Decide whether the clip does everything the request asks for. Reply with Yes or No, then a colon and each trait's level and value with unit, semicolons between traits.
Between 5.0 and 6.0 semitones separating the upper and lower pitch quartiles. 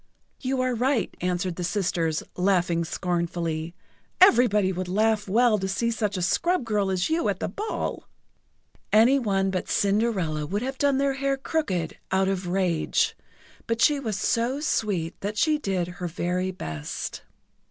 Yes: average, 5.3 semitones